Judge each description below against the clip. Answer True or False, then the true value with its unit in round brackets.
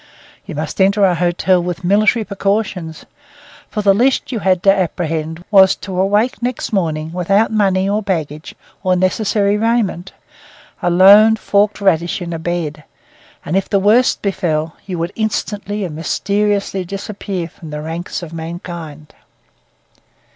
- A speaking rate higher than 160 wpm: False (145 wpm)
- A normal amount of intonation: True (3.3 semitones)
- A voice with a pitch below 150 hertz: False (190 Hz)